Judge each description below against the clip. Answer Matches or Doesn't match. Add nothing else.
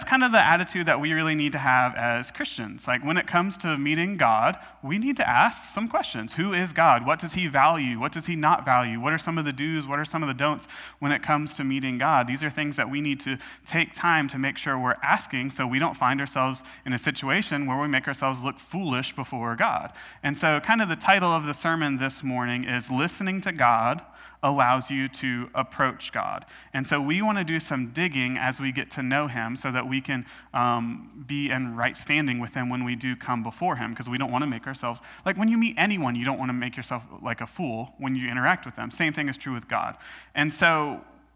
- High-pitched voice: Doesn't match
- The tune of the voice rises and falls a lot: Doesn't match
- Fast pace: Matches